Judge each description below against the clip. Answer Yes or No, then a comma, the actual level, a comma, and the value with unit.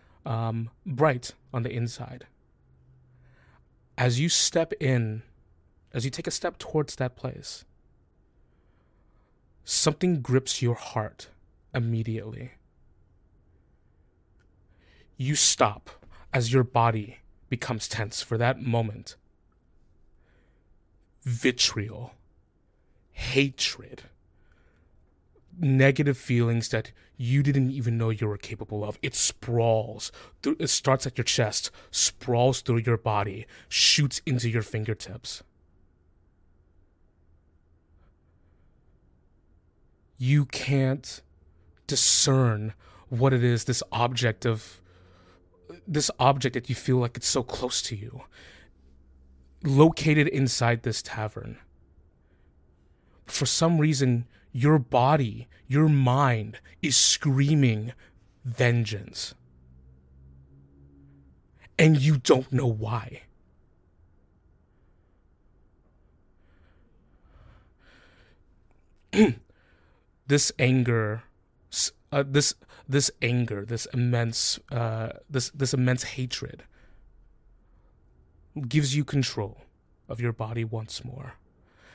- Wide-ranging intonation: Yes, wide, 6.8 semitones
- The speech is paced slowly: Yes, slow, 90 wpm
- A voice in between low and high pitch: No, low, 115 Hz